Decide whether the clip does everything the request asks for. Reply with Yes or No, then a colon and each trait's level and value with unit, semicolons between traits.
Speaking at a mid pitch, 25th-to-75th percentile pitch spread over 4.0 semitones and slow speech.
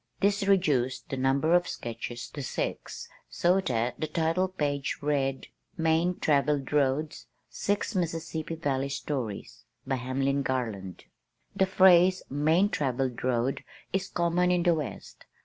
Yes: medium, 150 Hz; average, 4.8 semitones; slow, 130 wpm